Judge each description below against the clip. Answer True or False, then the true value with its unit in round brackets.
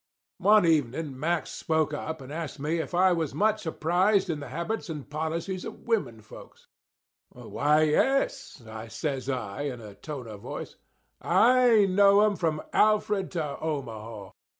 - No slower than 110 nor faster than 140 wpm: False (150 wpm)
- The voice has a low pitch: False (160 Hz)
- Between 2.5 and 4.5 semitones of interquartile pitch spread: False (5.5 semitones)